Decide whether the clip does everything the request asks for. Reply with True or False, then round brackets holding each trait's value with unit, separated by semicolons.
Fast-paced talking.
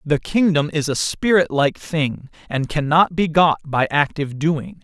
False (175 wpm)